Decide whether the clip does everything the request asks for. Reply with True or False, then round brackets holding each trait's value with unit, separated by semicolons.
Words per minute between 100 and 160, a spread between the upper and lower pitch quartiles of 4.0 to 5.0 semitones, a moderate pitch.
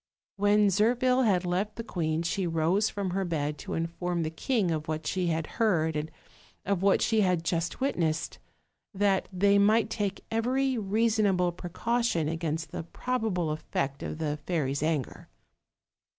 True (155 wpm; 4.6 semitones; 180 Hz)